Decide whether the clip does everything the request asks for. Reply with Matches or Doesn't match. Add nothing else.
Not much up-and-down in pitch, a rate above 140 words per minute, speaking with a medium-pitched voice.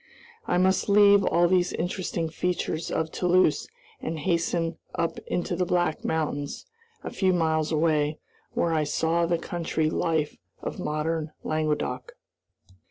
Doesn't match